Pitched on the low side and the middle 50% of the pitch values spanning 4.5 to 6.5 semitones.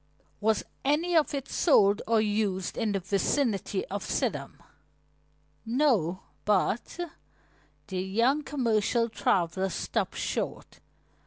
No: high, 215 Hz; average, 5.1 semitones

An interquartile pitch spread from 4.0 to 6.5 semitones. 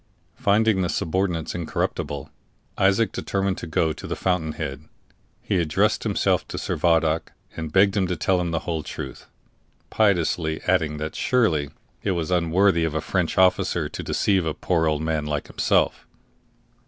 No: average, 3.2 semitones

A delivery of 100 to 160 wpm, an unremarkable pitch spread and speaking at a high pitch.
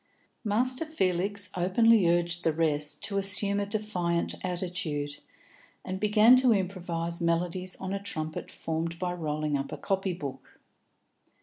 No: slow, 135 wpm; average, 3.3 semitones; medium, 180 Hz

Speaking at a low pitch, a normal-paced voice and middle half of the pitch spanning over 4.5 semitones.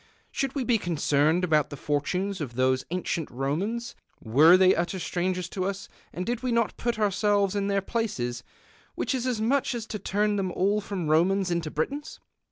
No: high, 190 Hz; average, 185 wpm; average, 5.2 semitones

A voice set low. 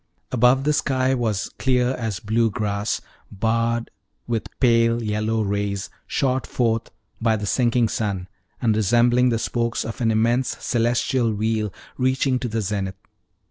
Yes: low, 115 Hz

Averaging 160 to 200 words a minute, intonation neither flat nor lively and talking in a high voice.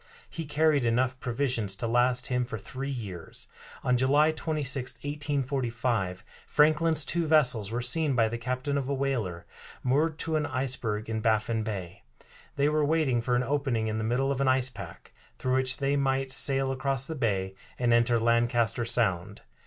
No: average, 175 wpm; average, 3.4 semitones; low, 130 Hz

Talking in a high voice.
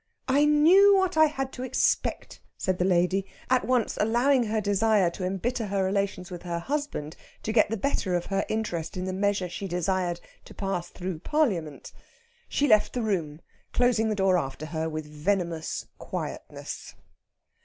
Yes: high, 195 Hz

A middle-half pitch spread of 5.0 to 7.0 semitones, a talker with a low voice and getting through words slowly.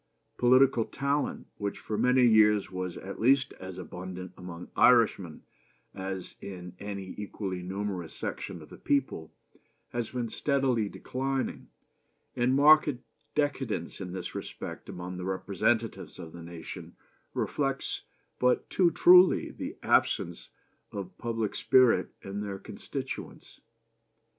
Yes: wide, 5.5 semitones; low, 105 Hz; slow, 125 wpm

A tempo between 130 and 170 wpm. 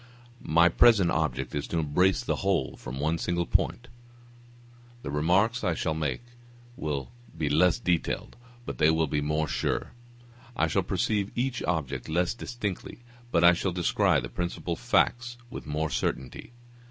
Yes: average, 155 wpm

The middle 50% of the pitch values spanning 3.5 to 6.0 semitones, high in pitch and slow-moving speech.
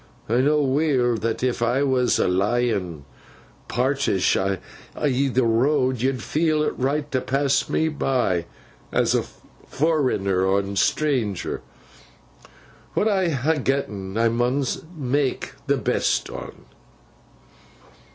No: average, 4.1 semitones; low, 130 Hz; slow, 120 wpm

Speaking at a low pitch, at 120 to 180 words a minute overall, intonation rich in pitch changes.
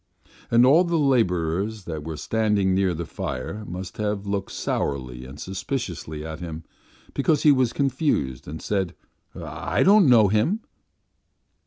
Yes: low, 100 Hz; average, 145 wpm; wide, 7.6 semitones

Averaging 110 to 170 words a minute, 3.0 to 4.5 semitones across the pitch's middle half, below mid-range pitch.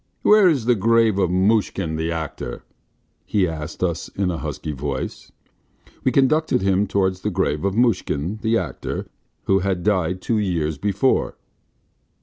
No: average, 150 wpm; average, 4.9 semitones; very low, 95 Hz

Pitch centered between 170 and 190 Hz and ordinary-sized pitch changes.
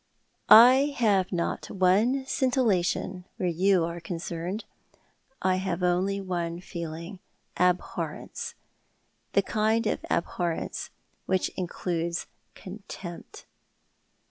Yes: medium, 185 Hz; average, 3.0 semitones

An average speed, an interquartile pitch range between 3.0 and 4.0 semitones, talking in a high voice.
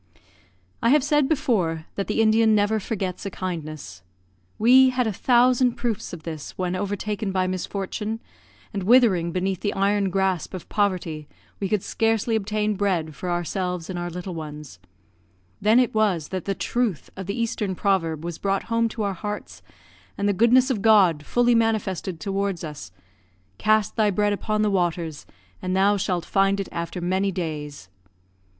Yes: average, 170 wpm; average, 3.6 semitones; high, 195 Hz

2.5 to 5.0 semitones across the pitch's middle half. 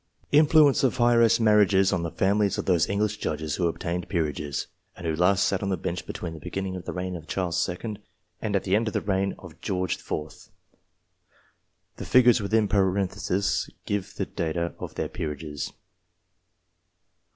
Yes: average, 3.4 semitones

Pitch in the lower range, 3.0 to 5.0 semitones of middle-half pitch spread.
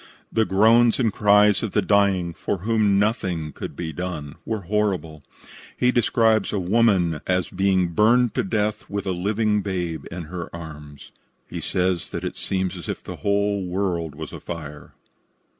Yes: very low, 95 Hz; average, 3.5 semitones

